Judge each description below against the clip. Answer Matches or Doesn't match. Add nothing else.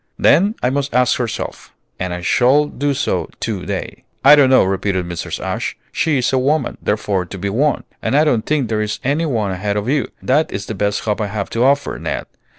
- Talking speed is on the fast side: Matches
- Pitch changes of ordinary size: Doesn't match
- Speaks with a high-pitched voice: Doesn't match